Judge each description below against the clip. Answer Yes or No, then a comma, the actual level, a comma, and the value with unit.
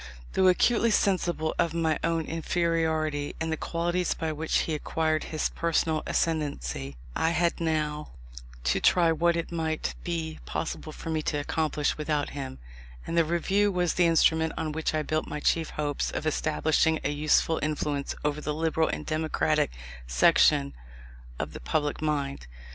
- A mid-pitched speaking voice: Yes, medium, 160 Hz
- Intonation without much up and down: Yes, narrow, 1.7 semitones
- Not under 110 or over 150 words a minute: No, average, 160 wpm